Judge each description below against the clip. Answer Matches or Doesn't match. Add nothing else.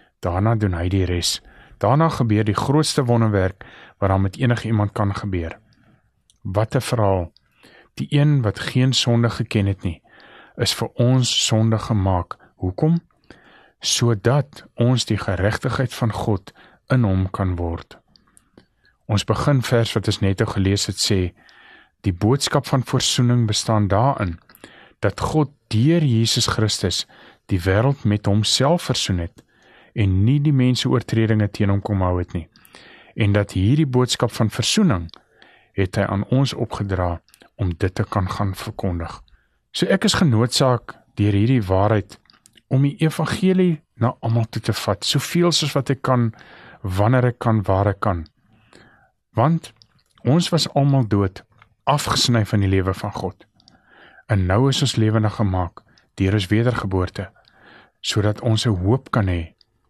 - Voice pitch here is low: Matches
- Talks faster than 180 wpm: Doesn't match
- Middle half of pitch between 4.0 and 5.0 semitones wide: Matches